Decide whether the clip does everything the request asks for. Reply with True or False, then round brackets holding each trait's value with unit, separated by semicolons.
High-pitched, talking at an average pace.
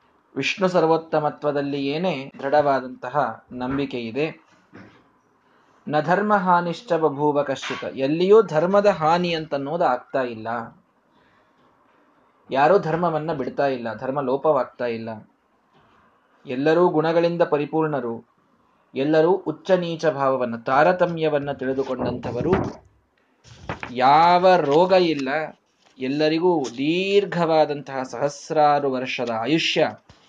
False (150 Hz; 80 wpm)